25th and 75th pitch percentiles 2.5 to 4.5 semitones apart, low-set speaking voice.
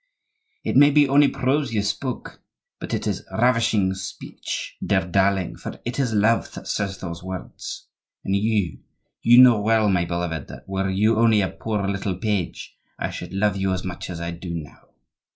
Yes: average, 3.7 semitones; low, 100 Hz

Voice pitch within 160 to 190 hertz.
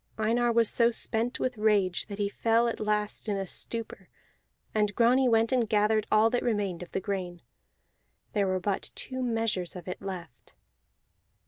No: high, 215 Hz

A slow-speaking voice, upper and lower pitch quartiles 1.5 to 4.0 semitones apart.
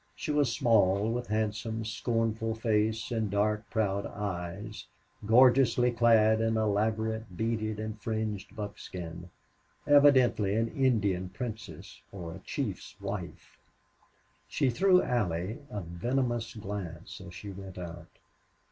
Yes: slow, 120 wpm; narrow, 2.6 semitones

